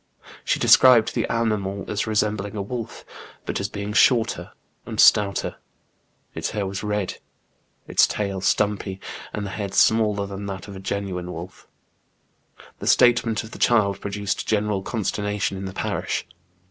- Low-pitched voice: Yes, low, 100 Hz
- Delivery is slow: No, average, 155 wpm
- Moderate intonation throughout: No, narrow, 1.6 semitones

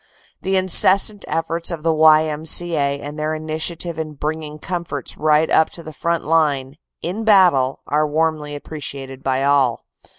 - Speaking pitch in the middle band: Yes, medium, 155 Hz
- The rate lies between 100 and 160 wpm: Yes, average, 145 wpm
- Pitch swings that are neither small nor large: No, narrow, 2.3 semitones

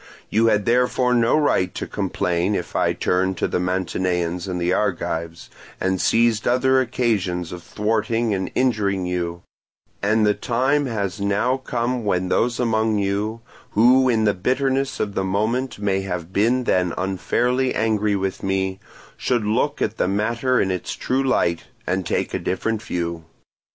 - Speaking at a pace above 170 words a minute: No, average, 160 wpm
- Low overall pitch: Yes, low, 105 Hz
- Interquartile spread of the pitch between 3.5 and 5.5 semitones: Yes, average, 4.3 semitones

